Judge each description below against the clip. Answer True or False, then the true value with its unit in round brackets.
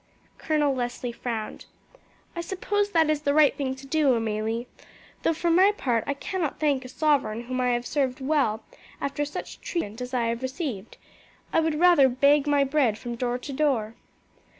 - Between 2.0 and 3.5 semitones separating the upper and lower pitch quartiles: False (4.1 semitones)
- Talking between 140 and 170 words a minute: False (180 wpm)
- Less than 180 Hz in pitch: False (270 Hz)